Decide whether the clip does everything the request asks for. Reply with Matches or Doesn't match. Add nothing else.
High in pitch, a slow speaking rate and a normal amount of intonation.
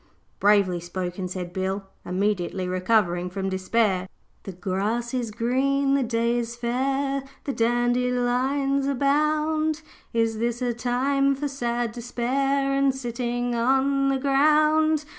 Matches